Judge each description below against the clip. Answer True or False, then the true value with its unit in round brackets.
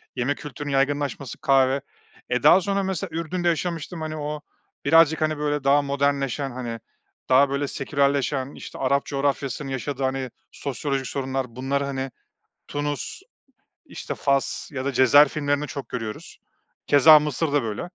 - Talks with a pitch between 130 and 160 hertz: True (140 Hz)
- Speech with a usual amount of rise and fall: False (1.8 semitones)